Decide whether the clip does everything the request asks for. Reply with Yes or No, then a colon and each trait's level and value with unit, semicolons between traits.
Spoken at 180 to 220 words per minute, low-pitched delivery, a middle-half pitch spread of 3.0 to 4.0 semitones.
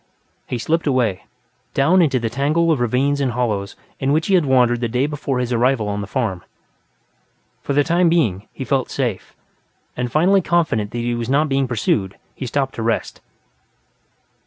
Yes: average, 185 wpm; low, 130 Hz; average, 3.7 semitones